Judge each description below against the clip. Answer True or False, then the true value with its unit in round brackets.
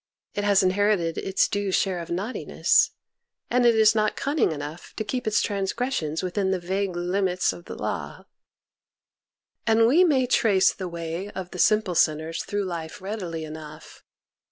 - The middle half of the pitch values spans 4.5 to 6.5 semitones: False (3.8 semitones)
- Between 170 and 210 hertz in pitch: True (190 Hz)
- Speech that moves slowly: False (165 wpm)